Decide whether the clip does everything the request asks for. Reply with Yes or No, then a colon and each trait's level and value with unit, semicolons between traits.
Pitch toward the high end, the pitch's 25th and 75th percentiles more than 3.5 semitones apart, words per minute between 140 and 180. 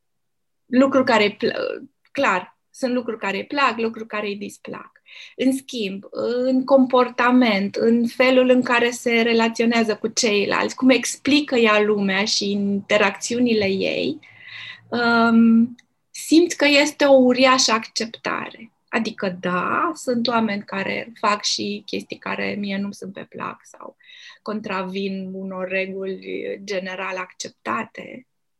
No: high, 230 Hz; average, 4.3 semitones; average, 125 wpm